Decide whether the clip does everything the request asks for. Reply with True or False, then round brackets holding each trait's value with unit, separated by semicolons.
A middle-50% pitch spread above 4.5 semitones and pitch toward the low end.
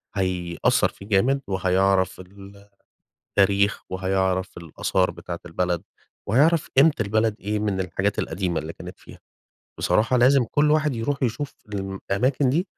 True (5.1 semitones; 100 Hz)